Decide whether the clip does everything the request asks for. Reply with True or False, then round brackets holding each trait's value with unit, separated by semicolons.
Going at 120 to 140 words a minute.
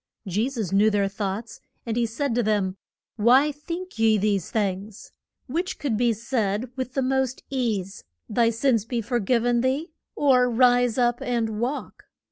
False (170 wpm)